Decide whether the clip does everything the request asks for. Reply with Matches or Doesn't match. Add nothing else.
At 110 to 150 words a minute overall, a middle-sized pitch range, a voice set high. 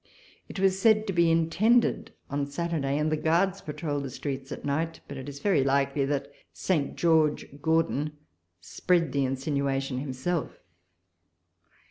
Doesn't match